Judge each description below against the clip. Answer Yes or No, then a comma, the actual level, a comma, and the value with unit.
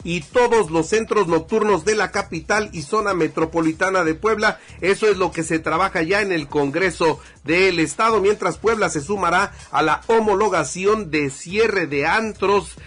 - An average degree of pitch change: Yes, average, 4.8 semitones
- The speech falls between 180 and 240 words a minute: No, average, 170 wpm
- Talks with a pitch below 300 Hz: Yes, high, 190 Hz